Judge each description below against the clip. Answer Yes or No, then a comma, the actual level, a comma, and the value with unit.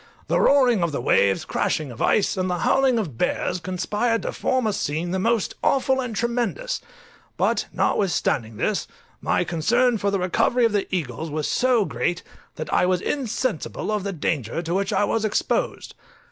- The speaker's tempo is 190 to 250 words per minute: No, average, 175 wpm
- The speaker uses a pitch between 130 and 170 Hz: No, high, 200 Hz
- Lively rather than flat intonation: Yes, wide, 5.9 semitones